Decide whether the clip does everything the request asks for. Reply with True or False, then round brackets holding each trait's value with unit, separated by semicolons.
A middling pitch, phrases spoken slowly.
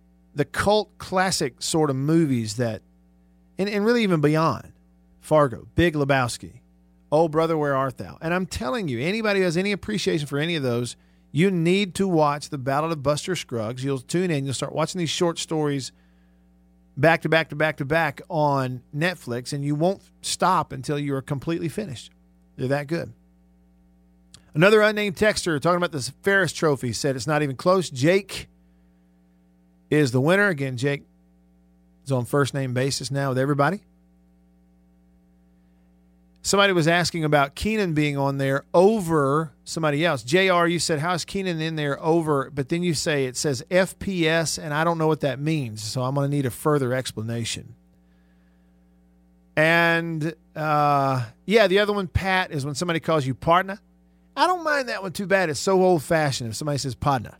False (145 Hz; 175 wpm)